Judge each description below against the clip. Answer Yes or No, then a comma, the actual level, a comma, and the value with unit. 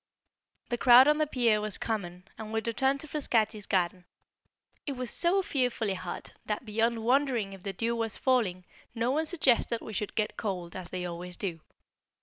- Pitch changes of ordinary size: Yes, average, 4.7 semitones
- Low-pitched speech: No, high, 225 Hz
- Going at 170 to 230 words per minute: Yes, average, 180 wpm